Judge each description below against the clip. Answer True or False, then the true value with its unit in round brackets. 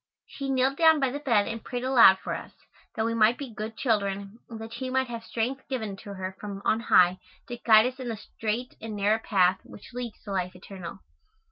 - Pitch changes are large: False (3.8 semitones)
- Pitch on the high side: True (225 Hz)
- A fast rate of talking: True (225 wpm)